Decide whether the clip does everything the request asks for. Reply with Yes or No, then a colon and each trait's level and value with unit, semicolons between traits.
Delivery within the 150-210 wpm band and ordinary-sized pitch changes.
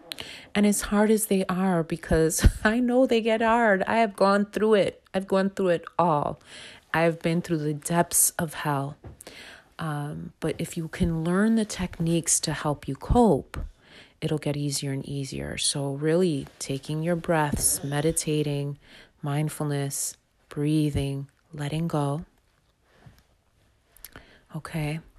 No: average, 140 wpm; average, 4.3 semitones